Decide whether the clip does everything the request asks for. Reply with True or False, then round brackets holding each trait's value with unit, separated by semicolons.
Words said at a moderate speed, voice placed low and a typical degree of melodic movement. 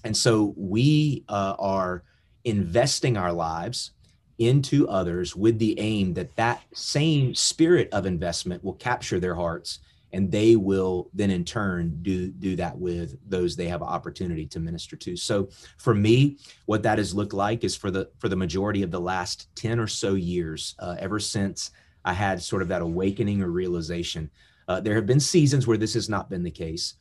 True (185 wpm; 95 Hz; 4.0 semitones)